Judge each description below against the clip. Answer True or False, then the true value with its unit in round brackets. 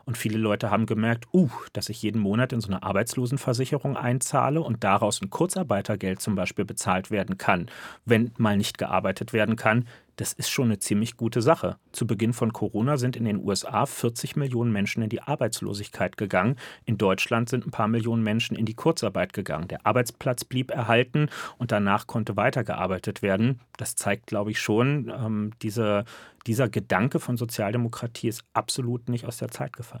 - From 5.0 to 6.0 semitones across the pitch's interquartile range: False (2.9 semitones)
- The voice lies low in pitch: True (115 Hz)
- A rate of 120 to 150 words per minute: False (180 wpm)